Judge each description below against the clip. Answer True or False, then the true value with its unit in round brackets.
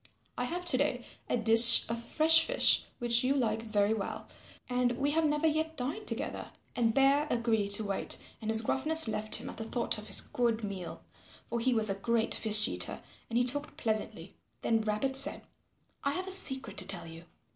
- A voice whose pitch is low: False (235 Hz)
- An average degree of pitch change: True (4.2 semitones)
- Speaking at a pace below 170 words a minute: False (200 wpm)